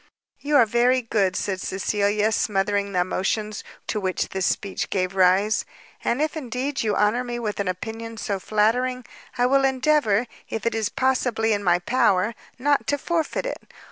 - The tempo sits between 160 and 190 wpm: Yes, average, 170 wpm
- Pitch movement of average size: Yes, average, 4.1 semitones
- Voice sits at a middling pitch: No, high, 220 Hz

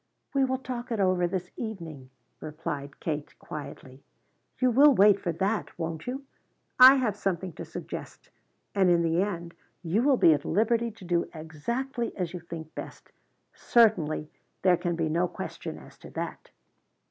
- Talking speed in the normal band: Yes, average, 165 wpm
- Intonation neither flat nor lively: No, wide, 6.1 semitones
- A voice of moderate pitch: Yes, medium, 180 Hz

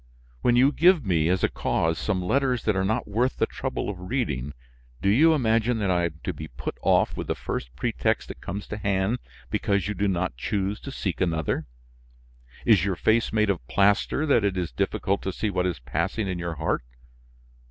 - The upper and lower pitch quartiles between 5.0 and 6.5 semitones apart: No, average, 4.1 semitones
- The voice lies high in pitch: No, low, 100 Hz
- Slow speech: No, fast, 205 wpm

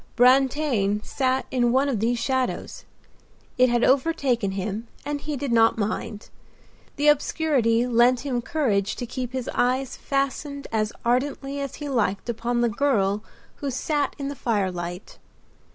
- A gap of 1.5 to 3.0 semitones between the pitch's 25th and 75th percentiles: No, average, 3.6 semitones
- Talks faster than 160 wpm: No, average, 150 wpm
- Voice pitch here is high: Yes, very high, 250 Hz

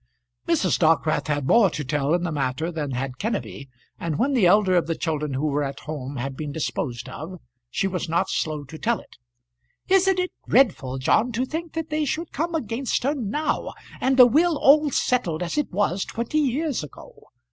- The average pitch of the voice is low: No, medium, 180 Hz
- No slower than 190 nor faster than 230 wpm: Yes, average, 200 wpm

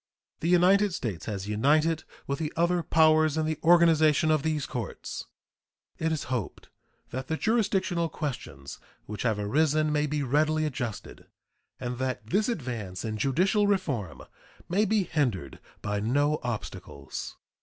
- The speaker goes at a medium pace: Yes, average, 145 wpm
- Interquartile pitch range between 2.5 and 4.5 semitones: No, wide, 5.4 semitones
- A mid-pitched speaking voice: Yes, medium, 150 Hz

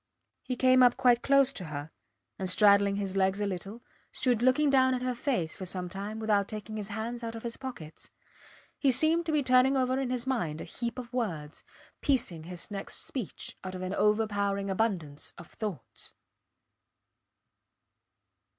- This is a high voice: Yes, high, 220 Hz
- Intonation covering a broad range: No, average, 4.8 semitones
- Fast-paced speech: No, average, 175 wpm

